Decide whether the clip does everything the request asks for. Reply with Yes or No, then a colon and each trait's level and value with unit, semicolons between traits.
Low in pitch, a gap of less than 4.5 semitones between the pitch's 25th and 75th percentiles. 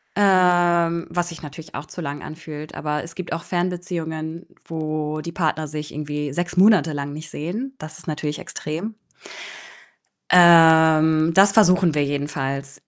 No: medium, 160 Hz; narrow, 2.6 semitones